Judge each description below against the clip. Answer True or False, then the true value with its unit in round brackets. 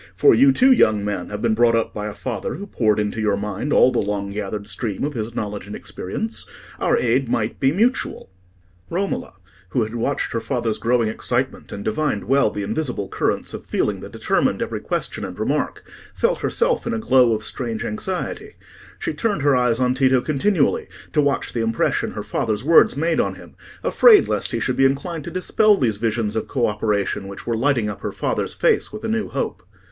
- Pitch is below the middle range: True (120 Hz)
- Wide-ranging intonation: True (5.8 semitones)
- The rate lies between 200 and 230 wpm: True (205 wpm)